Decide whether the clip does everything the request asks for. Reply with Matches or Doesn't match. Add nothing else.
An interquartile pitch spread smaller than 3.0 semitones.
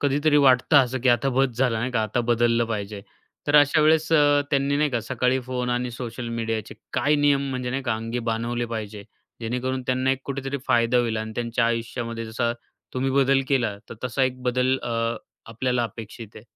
Matches